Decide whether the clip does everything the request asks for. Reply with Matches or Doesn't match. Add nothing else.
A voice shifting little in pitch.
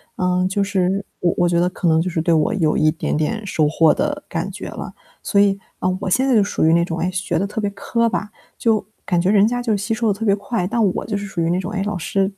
Doesn't match